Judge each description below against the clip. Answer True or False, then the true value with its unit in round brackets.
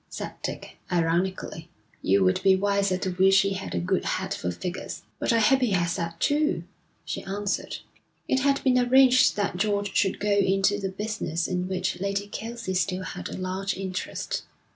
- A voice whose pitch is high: True (195 Hz)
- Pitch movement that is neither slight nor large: False (2.2 semitones)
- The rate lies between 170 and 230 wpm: True (185 wpm)